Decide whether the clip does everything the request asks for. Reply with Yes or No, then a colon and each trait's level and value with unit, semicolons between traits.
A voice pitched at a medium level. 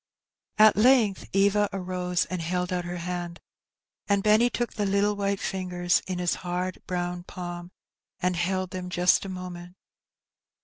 Yes: medium, 180 Hz